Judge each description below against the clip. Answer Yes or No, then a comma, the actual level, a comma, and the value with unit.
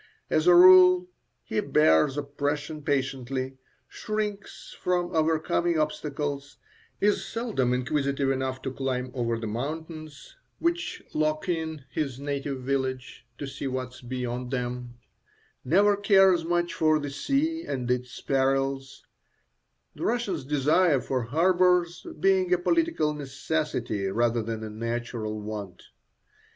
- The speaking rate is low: Yes, slow, 125 wpm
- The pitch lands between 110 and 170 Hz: Yes, medium, 140 Hz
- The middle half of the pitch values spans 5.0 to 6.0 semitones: Yes, average, 5.3 semitones